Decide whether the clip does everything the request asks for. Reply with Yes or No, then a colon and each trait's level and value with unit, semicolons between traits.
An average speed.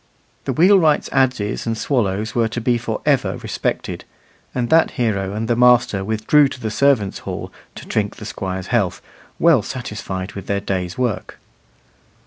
Yes: average, 160 wpm